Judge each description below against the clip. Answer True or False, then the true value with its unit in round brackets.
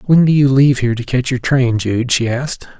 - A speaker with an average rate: False (260 wpm)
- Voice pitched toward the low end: True (125 Hz)